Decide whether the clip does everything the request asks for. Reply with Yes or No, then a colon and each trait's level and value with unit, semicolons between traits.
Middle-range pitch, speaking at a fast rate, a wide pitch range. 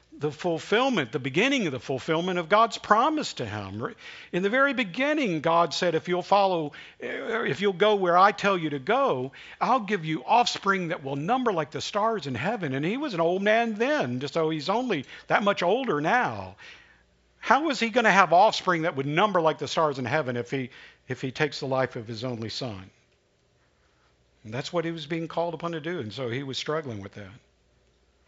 Yes: medium, 160 Hz; fast, 210 wpm; wide, 6.7 semitones